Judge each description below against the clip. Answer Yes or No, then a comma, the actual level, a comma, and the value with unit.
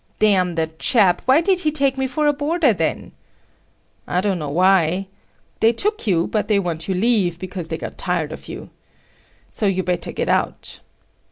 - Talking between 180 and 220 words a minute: Yes, average, 185 wpm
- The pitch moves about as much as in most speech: No, wide, 7.0 semitones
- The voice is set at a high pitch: Yes, high, 195 Hz